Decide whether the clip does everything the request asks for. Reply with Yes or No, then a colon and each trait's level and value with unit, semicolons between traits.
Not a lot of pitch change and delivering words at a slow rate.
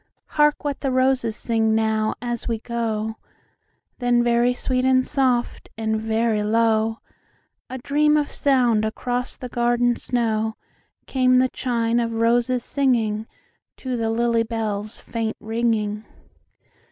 Yes: narrow, 2.3 semitones; slow, 115 wpm